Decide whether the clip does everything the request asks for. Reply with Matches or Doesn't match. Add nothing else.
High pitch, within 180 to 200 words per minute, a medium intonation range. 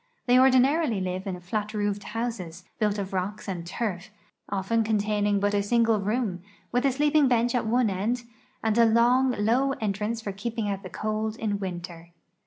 Matches